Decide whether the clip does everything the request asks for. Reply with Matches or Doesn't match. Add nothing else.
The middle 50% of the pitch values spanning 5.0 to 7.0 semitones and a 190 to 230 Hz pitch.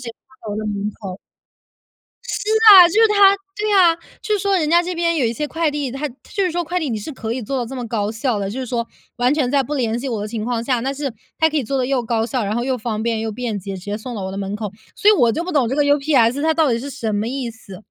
Doesn't match